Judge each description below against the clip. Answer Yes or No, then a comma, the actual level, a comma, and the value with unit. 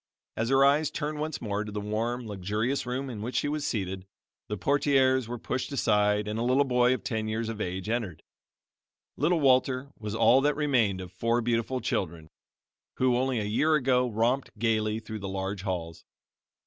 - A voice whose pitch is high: No, low, 115 Hz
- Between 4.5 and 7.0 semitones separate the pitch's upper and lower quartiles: No, average, 3.9 semitones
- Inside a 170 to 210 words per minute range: Yes, average, 185 wpm